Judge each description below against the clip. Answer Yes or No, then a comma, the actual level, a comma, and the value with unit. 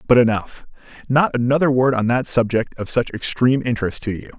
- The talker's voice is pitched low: Yes, low, 120 Hz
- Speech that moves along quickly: No, average, 190 wpm